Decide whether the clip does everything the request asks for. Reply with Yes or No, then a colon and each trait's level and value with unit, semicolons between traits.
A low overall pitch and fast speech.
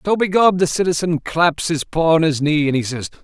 No: medium, 160 Hz; fast, 240 wpm